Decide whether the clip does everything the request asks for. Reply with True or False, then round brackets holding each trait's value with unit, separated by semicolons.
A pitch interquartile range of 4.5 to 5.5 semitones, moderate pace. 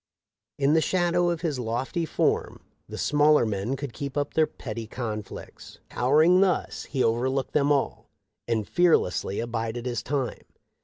True (4.9 semitones; 150 wpm)